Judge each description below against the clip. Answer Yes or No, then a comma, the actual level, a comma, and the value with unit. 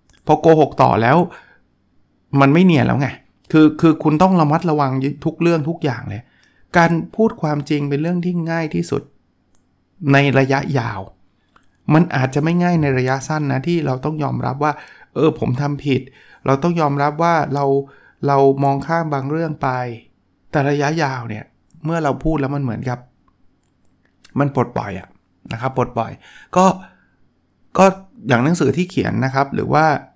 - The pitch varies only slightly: No, average, 3.8 semitones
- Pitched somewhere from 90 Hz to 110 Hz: No, medium, 140 Hz